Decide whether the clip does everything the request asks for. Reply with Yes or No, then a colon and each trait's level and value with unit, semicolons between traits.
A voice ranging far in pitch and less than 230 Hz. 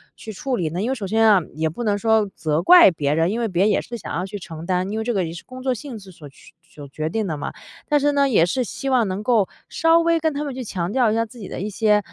Yes: wide, 6.1 semitones; high, 210 Hz